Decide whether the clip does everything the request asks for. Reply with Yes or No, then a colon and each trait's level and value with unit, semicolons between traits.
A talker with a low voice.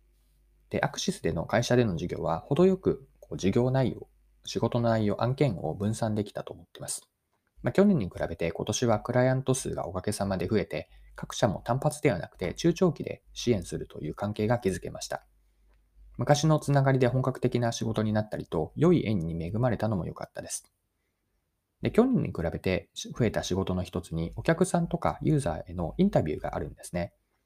Yes: low, 110 Hz